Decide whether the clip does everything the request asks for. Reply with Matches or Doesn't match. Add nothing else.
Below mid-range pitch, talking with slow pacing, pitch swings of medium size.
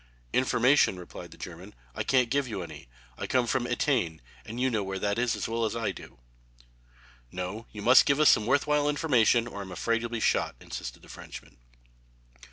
Doesn't match